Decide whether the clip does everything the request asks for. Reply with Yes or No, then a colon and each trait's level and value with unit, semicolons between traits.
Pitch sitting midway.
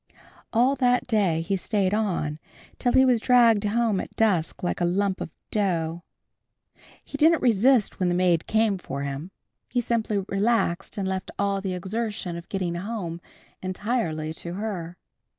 No: high, 195 Hz